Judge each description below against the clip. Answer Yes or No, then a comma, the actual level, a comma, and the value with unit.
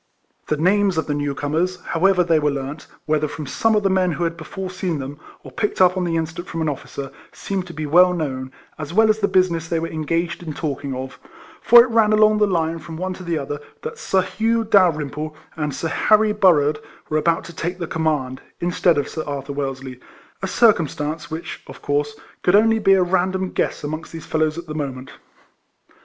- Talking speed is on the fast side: Yes, fast, 215 wpm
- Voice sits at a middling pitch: Yes, medium, 165 Hz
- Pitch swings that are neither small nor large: Yes, average, 4.0 semitones